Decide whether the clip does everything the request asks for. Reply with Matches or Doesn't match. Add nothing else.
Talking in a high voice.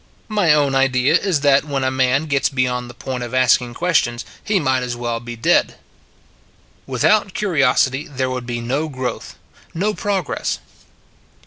Doesn't match